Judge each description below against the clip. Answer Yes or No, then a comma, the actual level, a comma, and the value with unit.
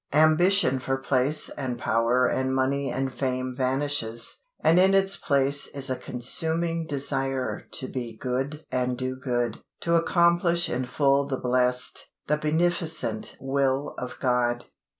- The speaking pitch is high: No, low, 135 Hz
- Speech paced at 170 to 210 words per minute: No, average, 140 wpm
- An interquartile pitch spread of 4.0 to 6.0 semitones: No, average, 3.2 semitones